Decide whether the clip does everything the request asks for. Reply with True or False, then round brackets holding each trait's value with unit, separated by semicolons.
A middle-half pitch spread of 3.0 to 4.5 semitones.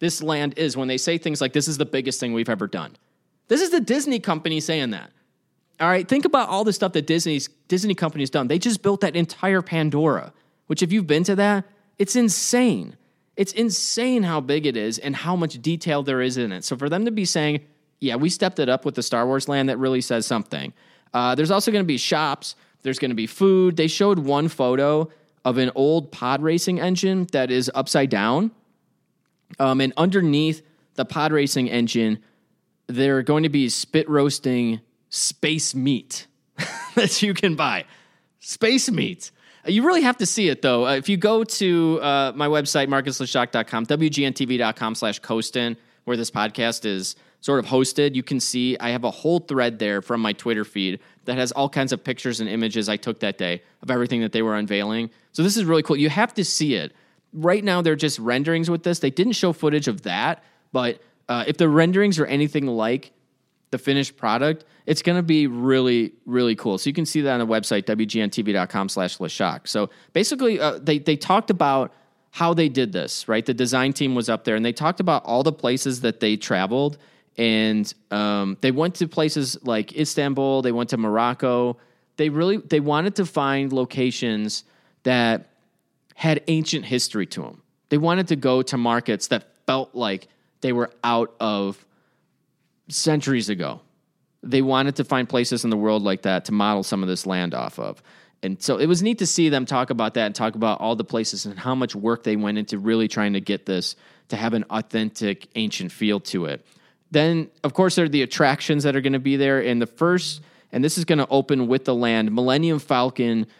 False (5.4 semitones)